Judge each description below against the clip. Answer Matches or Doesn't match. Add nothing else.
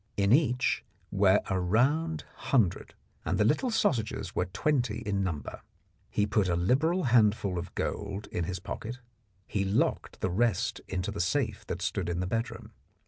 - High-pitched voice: Doesn't match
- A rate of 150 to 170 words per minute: Matches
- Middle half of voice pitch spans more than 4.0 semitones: Matches